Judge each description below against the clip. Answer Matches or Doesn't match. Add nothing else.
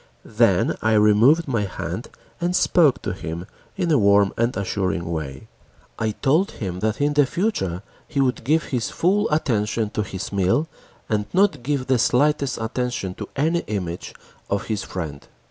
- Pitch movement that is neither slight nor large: Doesn't match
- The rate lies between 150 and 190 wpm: Matches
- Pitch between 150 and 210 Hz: Doesn't match